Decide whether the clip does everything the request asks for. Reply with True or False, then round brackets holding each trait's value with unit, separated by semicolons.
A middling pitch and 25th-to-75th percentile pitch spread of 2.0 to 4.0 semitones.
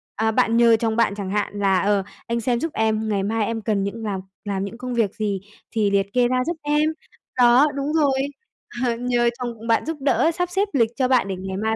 False (230 Hz; 3.7 semitones)